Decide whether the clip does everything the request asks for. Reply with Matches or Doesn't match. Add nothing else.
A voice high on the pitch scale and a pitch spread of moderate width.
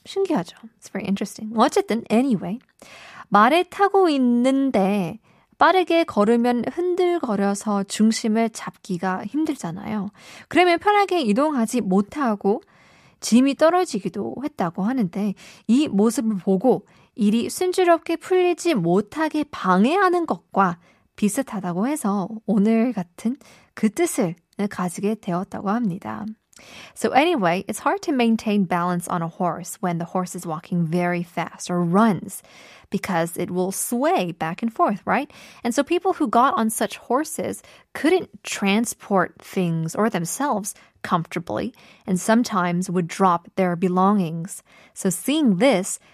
Doesn't match